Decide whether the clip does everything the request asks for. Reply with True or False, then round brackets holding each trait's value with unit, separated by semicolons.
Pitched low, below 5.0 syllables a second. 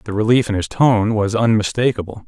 False (105 Hz; 5.4 syllables/s)